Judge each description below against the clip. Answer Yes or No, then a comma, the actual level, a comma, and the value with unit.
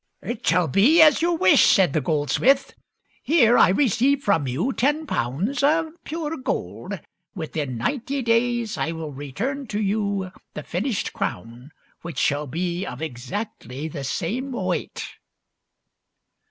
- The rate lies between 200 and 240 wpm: No, average, 145 wpm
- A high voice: Yes, high, 200 Hz